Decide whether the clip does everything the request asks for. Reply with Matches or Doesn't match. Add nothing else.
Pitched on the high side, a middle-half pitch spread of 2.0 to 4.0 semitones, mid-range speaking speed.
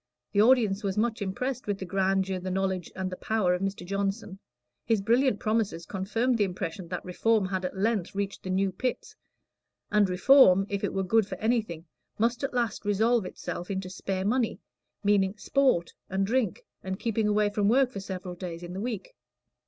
Matches